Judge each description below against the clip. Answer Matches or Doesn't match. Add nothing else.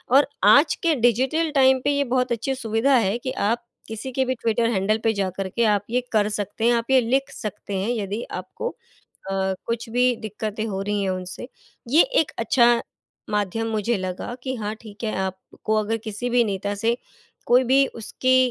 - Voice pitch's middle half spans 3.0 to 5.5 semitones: Matches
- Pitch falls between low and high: Doesn't match